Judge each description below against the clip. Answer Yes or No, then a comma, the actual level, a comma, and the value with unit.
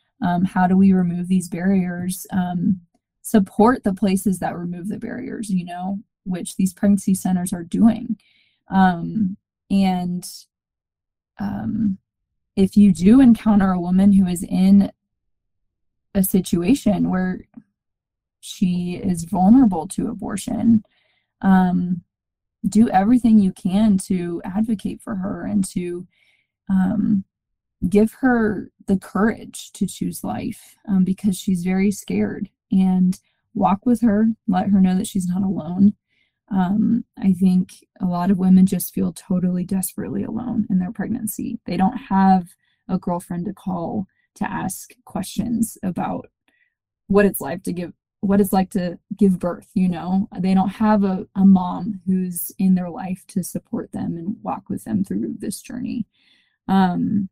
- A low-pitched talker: No, high, 195 Hz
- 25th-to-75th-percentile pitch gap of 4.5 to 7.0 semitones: No, narrow, 2.6 semitones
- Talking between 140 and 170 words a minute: Yes, average, 145 wpm